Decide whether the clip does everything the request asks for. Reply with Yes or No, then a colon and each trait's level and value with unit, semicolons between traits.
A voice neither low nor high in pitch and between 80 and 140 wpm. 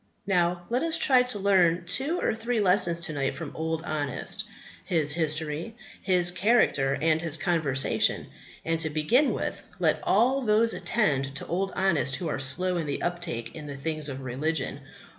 No: medium, 170 Hz; average, 175 wpm